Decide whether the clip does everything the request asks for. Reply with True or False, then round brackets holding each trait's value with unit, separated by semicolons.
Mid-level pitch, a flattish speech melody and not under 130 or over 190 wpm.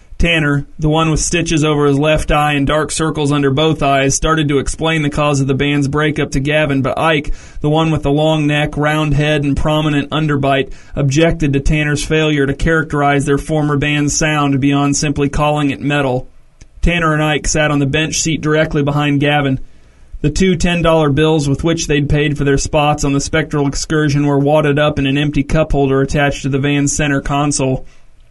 False (145 Hz; 1.5 semitones; 200 wpm)